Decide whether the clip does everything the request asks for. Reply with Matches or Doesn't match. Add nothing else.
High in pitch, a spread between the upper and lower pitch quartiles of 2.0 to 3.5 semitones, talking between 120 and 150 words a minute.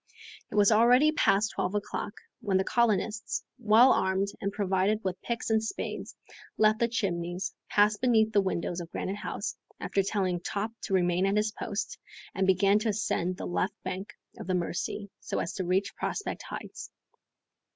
Doesn't match